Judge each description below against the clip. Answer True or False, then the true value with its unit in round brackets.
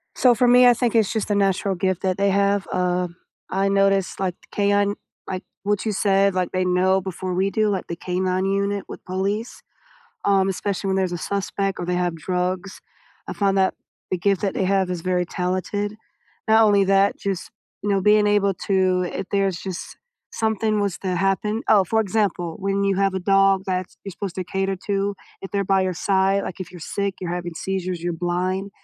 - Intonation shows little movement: True (1.5 semitones)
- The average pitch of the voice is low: False (195 Hz)